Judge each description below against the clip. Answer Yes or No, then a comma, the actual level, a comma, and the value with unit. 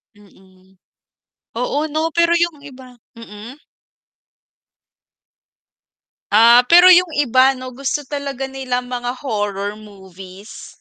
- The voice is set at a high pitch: Yes, very high, 250 Hz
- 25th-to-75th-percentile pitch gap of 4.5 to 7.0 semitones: Yes, average, 5.2 semitones